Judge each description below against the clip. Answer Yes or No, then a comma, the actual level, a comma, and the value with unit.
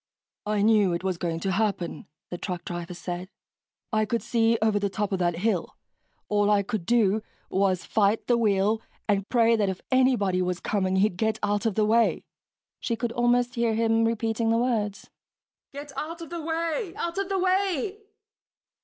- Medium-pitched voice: No, high, 220 Hz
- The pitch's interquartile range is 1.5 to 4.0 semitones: Yes, average, 3.7 semitones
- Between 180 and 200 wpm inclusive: Yes, average, 185 wpm